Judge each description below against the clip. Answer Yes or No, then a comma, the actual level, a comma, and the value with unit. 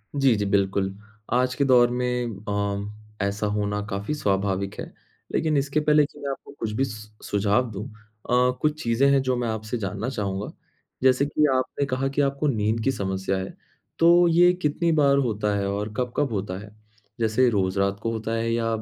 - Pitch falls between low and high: No, low, 115 Hz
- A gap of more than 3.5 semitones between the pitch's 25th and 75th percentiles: Yes, average, 4.9 semitones